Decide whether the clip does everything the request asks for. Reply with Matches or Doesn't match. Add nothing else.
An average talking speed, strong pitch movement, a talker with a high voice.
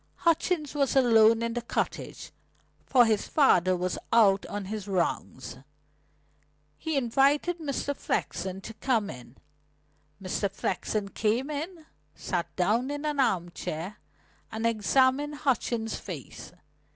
Doesn't match